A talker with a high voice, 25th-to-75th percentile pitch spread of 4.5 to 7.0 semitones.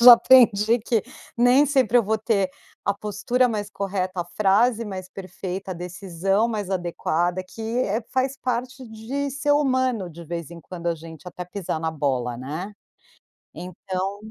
Yes: high, 200 Hz; average, 5.0 semitones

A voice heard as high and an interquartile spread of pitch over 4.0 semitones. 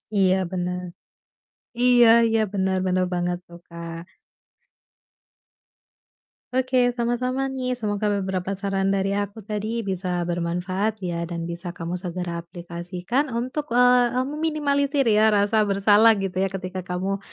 Yes: high, 195 Hz; average, 4.6 semitones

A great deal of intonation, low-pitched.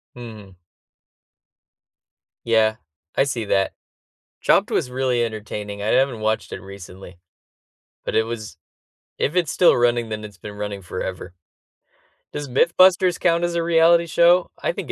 Yes: wide, 7.9 semitones; low, 115 Hz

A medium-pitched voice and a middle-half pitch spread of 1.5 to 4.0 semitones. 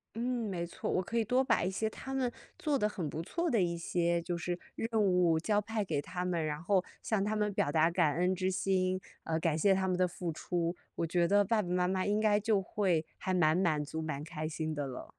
Yes: medium, 180 Hz; average, 3.7 semitones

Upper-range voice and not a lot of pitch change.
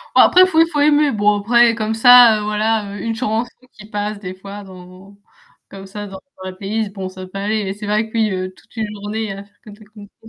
Yes: high, 210 Hz; narrow, 2.2 semitones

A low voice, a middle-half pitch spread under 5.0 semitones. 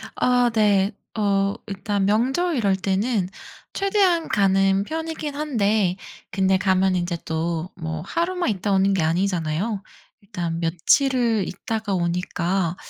No: high, 195 Hz; average, 4.2 semitones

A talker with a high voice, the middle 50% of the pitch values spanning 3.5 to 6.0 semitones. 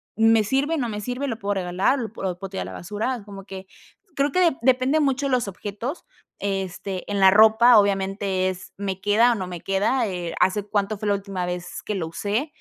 Yes: high, 205 Hz; average, 4.1 semitones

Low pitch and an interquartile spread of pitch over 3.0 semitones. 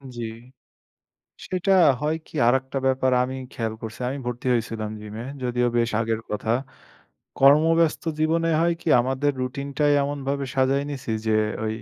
Yes: low, 130 Hz; average, 3.9 semitones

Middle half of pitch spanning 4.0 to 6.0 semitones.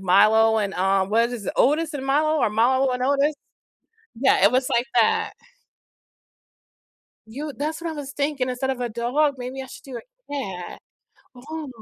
Yes: average, 4.3 semitones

